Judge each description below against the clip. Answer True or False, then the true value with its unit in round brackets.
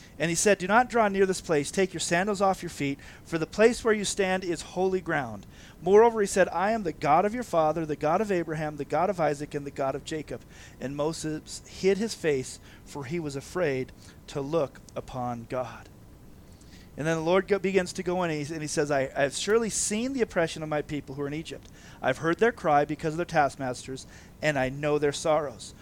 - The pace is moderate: False (230 wpm)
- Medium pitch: True (155 Hz)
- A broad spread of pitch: True (5.9 semitones)